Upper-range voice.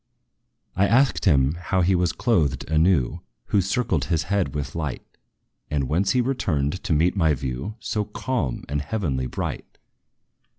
No: very low, 85 Hz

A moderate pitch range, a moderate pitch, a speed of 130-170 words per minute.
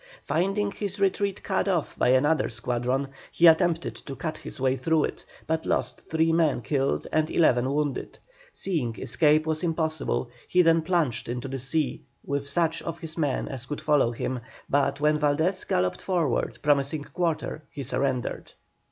Yes: average, 3.6 semitones; medium, 150 Hz; average, 165 wpm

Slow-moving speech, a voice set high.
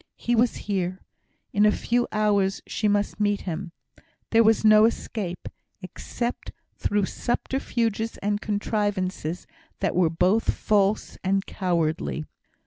Yes: slow, 125 wpm; high, 205 Hz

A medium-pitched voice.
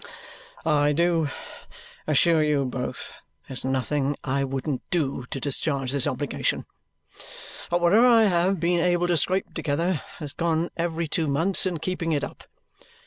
Yes: medium, 160 Hz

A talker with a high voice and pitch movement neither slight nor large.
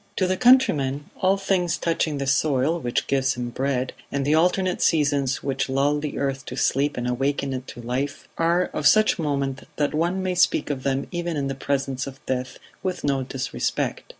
No: medium, 140 Hz; average, 3.9 semitones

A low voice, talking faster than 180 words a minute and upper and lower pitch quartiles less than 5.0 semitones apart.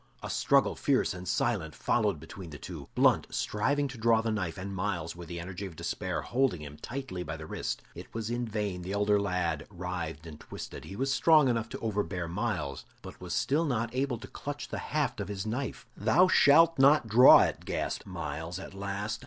No: low, 105 Hz; fast, 205 wpm; wide, 5.4 semitones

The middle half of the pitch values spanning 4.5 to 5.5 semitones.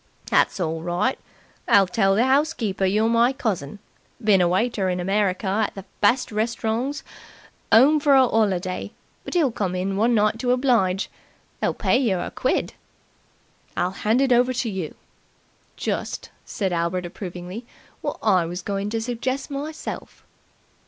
Yes: average, 4.8 semitones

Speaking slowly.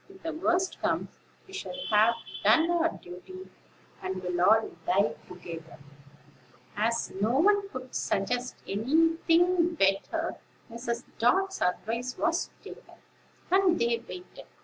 Yes: slow, 125 wpm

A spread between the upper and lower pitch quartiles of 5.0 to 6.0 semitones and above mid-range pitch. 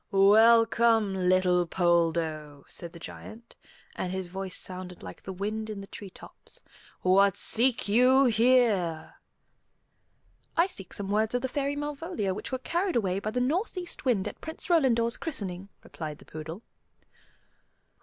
Yes: average, 5.3 semitones; high, 205 Hz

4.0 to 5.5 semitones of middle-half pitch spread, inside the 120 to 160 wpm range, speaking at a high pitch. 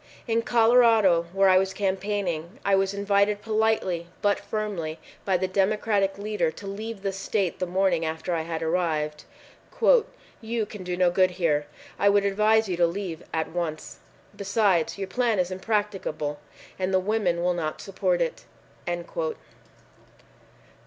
No: average, 3.2 semitones; average, 150 wpm; high, 195 Hz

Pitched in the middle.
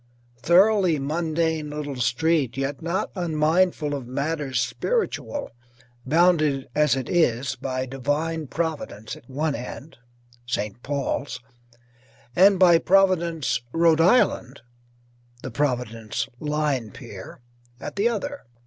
Yes: medium, 150 Hz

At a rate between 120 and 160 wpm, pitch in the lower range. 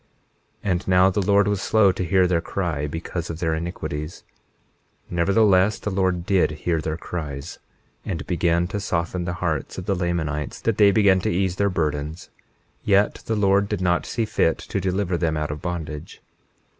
No: average, 180 wpm; very low, 90 Hz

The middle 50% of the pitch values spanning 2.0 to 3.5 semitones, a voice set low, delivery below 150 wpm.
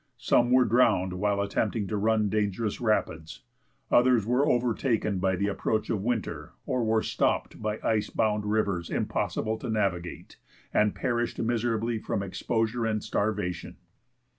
Yes: narrow, 2.6 semitones; low, 110 Hz; average, 140 wpm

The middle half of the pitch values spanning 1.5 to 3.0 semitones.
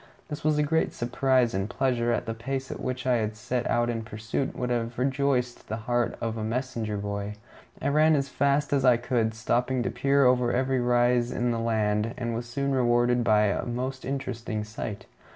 Yes: narrow, 2.5 semitones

